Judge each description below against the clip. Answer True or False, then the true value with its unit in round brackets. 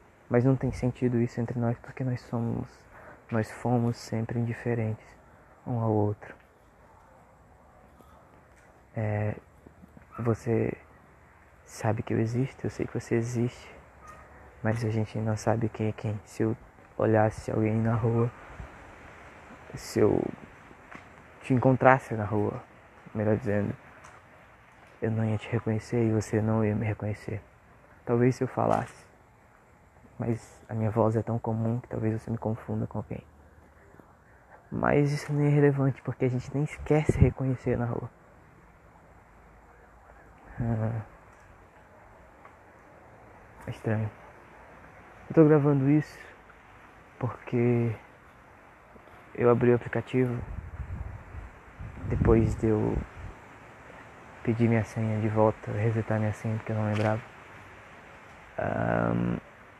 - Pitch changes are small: True (2.3 semitones)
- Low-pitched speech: True (110 Hz)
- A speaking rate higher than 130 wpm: False (120 wpm)